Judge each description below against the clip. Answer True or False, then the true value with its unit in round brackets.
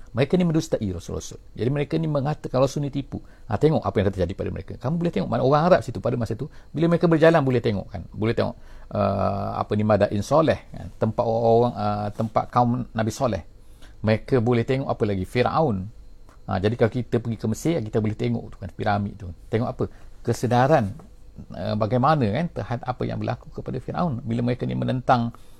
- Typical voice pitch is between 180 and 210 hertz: False (115 Hz)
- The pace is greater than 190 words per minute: True (200 wpm)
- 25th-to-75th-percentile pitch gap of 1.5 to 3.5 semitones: False (4.3 semitones)